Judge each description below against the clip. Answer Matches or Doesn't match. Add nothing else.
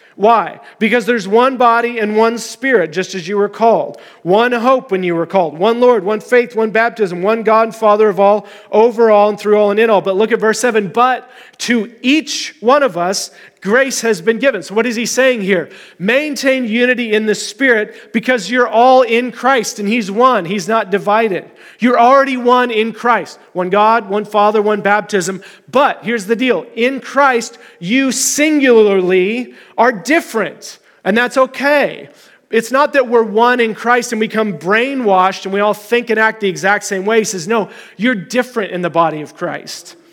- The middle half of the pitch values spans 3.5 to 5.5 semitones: Doesn't match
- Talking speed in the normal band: Matches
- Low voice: Doesn't match